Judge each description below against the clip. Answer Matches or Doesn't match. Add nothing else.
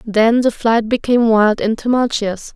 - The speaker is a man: Doesn't match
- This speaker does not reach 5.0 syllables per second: Matches